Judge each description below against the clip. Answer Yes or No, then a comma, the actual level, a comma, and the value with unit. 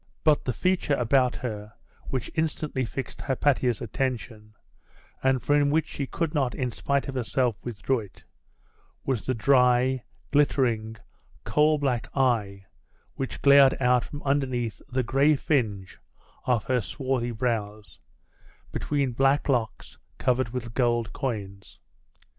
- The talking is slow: Yes, slow, 130 wpm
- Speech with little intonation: No, average, 3.1 semitones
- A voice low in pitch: Yes, low, 125 Hz